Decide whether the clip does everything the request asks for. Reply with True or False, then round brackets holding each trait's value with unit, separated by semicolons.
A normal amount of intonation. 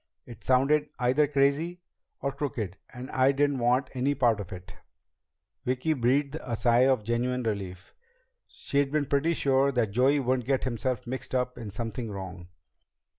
True (3.0 semitones)